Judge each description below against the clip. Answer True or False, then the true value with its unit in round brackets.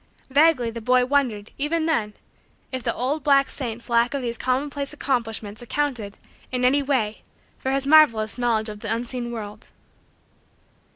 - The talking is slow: False (155 wpm)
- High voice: True (250 Hz)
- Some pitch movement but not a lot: True (3.6 semitones)